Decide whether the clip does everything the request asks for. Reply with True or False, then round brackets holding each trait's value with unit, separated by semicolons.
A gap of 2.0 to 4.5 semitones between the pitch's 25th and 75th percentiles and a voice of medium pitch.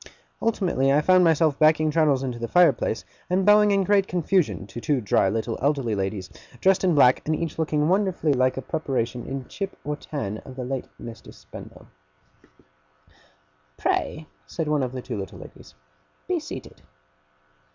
False (5.4 semitones; 150 Hz)